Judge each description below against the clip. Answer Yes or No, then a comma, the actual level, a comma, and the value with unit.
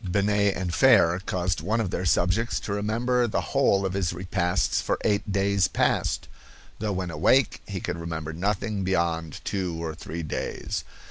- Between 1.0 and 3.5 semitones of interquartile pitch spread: Yes, average, 3.2 semitones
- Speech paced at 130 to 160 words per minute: No, average, 170 wpm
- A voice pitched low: Yes, very low, 95 Hz